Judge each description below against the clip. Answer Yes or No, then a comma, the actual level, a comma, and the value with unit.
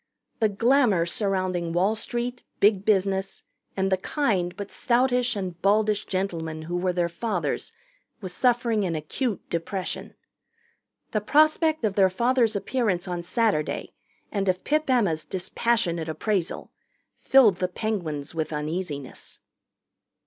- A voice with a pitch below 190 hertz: No, high, 195 Hz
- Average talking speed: No, slow, 125 wpm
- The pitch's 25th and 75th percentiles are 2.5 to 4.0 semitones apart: No, average, 4.8 semitones